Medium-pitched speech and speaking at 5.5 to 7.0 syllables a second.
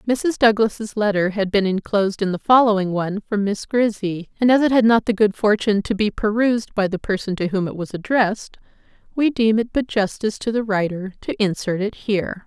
No: high, 210 Hz; 5.6 syllables/s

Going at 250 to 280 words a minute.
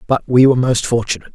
No: fast, 225 wpm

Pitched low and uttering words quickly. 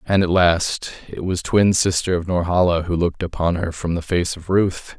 Yes: very low, 90 Hz; fast, 215 wpm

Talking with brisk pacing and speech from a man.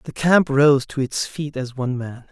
Yes: fast, 235 wpm; male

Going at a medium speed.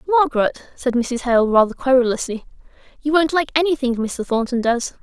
Yes: average, 155 wpm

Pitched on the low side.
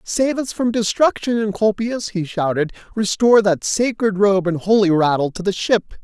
No: high, 205 Hz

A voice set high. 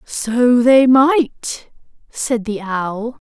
Yes: high, 240 Hz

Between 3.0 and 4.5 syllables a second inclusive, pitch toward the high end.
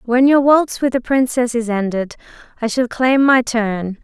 Yes: 4.3 syllables/s; high, 240 Hz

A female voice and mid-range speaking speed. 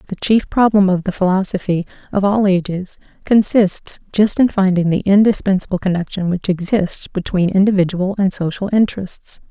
Yes: female; average, 145 wpm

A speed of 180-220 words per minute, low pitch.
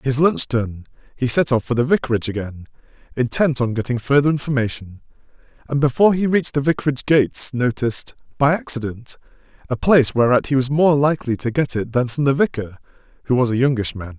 Yes: average, 185 wpm; low, 130 Hz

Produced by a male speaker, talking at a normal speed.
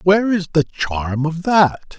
Yes: male; average, 180 wpm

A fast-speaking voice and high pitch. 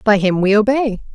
Yes: fast, 210 wpm; high, 215 Hz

